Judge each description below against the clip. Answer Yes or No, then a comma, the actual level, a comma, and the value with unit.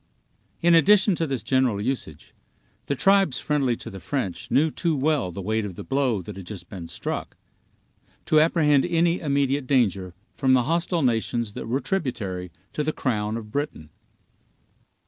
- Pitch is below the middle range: Yes, low, 130 Hz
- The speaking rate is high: No, average, 165 wpm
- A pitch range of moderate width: No, wide, 6.5 semitones